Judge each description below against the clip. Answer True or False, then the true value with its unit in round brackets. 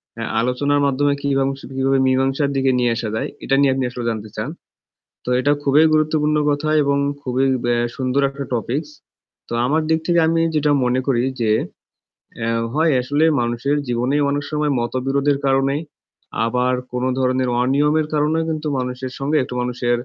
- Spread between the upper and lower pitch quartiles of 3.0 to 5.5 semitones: False (2.6 semitones)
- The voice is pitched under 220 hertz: True (135 Hz)